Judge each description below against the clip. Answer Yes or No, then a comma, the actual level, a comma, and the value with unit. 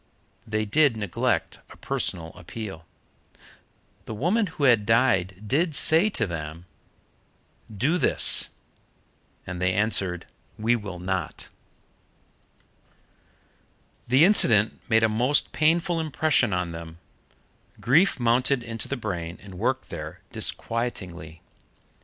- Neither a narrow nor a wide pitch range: No, wide, 7.2 semitones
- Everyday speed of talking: No, slow, 110 wpm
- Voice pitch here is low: Yes, low, 110 Hz